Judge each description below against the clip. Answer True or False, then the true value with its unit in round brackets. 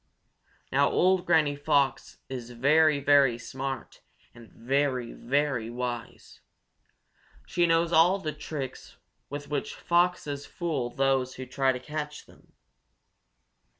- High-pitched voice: False (140 Hz)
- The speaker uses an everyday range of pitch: True (3.0 semitones)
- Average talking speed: False (115 wpm)